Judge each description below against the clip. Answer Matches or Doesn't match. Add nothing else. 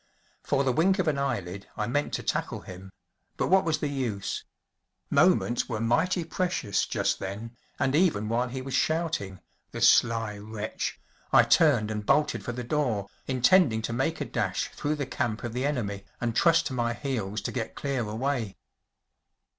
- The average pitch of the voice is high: Doesn't match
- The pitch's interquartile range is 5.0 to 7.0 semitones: Matches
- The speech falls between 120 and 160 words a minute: Doesn't match